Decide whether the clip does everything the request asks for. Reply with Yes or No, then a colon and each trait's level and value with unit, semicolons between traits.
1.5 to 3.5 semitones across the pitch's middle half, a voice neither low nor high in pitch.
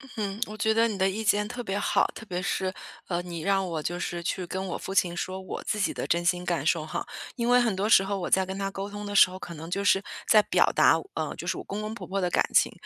No: narrow, 2.6 semitones; high, 195 Hz